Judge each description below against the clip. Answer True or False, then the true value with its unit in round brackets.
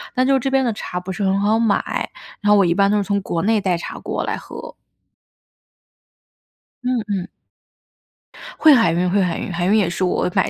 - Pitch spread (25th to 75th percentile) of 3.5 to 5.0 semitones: True (3.8 semitones)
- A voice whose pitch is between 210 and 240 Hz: False (200 Hz)